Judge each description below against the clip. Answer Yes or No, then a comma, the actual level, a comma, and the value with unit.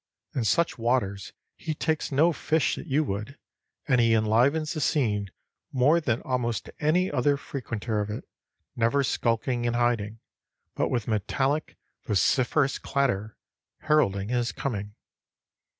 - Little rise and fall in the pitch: No, average, 4.5 semitones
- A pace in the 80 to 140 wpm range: Yes, slow, 135 wpm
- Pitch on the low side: Yes, low, 125 Hz